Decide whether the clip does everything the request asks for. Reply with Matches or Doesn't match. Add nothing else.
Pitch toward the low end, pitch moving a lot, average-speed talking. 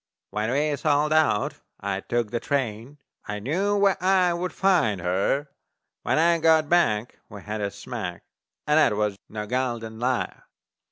Matches